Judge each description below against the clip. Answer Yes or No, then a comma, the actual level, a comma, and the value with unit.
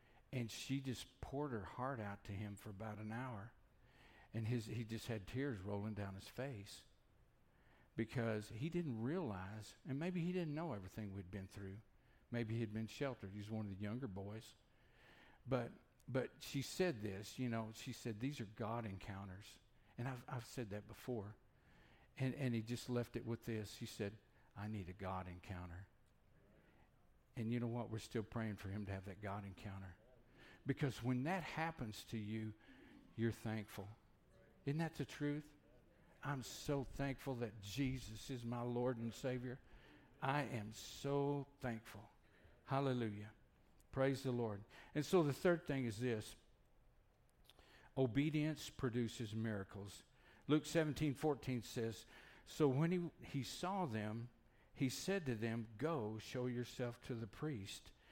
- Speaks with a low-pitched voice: Yes, low, 115 Hz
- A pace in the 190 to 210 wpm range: No, average, 160 wpm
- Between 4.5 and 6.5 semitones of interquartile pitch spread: No, average, 3.9 semitones